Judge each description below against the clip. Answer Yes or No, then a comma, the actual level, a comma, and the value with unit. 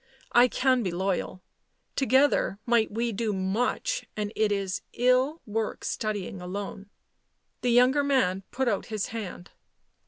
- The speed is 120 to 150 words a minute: Yes, slow, 135 wpm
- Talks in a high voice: Yes, high, 220 Hz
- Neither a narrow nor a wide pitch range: Yes, average, 4.3 semitones